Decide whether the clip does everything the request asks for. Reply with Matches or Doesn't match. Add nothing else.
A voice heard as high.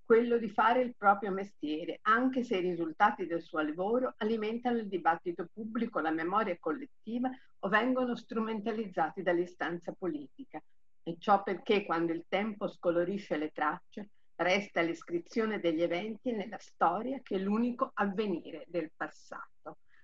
Matches